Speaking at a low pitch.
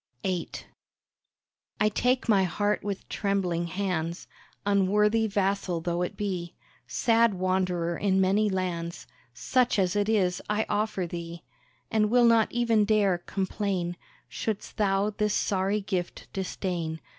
No: high, 195 Hz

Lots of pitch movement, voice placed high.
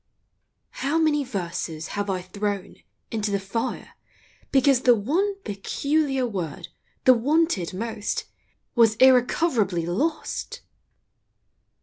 Yes: wide, 6.0 semitones; high, 230 Hz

